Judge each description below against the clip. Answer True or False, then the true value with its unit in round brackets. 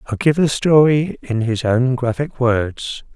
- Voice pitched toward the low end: True (125 Hz)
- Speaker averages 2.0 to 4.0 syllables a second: True (3.9 syllables/s)